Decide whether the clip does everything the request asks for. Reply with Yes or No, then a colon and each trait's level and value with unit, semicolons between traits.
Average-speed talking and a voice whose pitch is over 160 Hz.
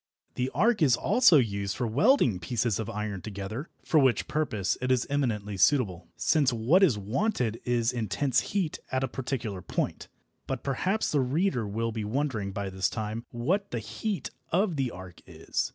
No: average, 175 wpm; low, 125 Hz